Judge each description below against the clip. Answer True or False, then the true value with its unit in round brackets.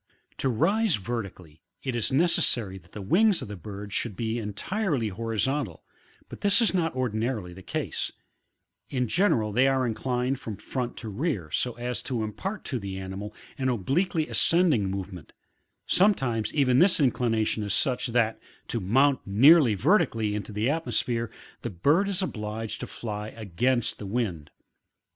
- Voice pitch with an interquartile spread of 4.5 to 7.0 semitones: True (4.9 semitones)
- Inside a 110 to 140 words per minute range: False (155 wpm)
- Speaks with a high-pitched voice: False (120 Hz)